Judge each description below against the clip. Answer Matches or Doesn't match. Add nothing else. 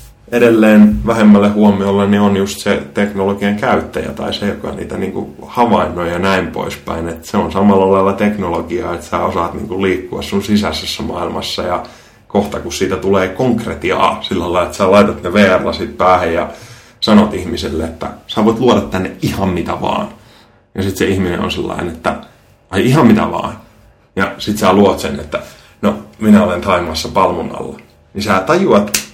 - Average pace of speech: Doesn't match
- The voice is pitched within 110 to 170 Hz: Doesn't match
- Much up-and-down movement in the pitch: Doesn't match